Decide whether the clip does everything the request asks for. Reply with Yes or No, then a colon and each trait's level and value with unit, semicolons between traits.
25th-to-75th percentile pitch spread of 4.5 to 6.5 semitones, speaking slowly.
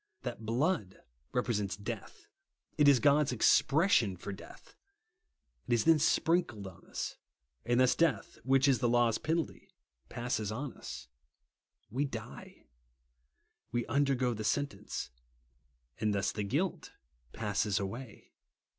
Yes: average, 5.0 semitones; slow, 130 wpm